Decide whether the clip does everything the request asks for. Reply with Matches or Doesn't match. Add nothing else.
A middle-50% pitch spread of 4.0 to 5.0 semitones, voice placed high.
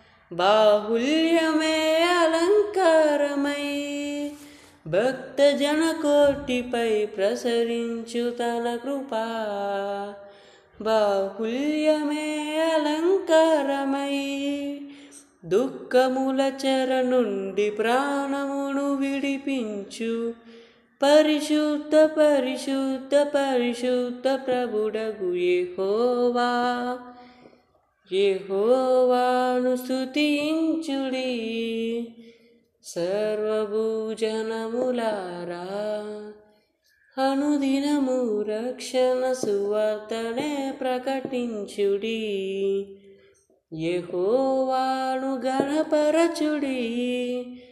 Matches